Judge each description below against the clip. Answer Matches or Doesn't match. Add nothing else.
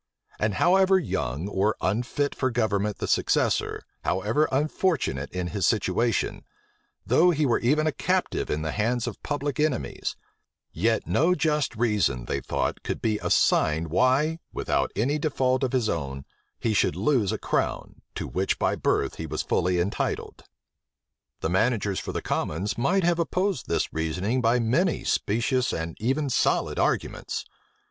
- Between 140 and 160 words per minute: Matches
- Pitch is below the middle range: Matches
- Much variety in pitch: Matches